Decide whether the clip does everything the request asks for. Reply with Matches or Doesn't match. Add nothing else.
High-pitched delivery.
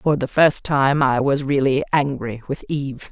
Doesn't match